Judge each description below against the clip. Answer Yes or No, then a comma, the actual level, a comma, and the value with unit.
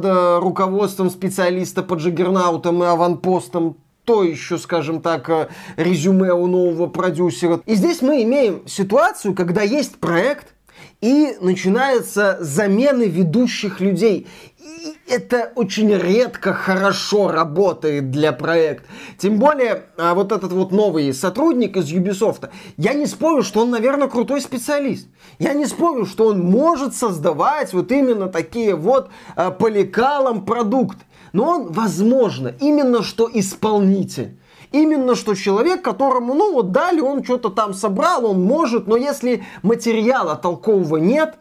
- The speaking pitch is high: Yes, high, 205 Hz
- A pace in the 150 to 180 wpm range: No, average, 130 wpm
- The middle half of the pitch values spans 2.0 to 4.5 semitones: No, wide, 5.5 semitones